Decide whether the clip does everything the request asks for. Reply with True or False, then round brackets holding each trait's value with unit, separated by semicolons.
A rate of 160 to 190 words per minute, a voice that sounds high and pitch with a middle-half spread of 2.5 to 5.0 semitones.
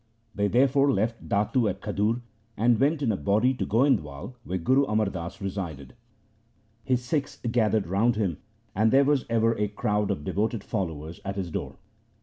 False (170 wpm; 105 Hz; 4.1 semitones)